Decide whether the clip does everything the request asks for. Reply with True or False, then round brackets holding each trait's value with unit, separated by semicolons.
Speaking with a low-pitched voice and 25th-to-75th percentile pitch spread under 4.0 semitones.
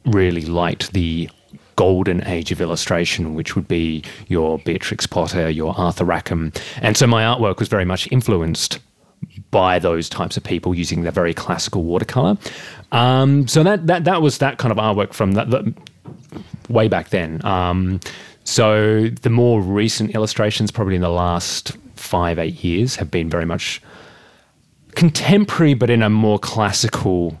False (105 Hz; 5.4 semitones)